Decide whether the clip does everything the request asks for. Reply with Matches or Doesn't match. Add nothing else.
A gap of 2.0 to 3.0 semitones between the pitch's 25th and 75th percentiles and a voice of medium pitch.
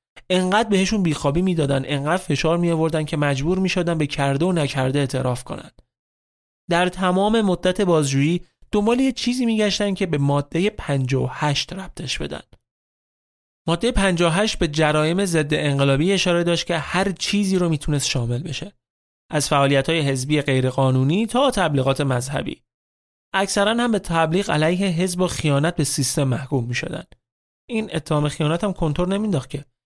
Doesn't match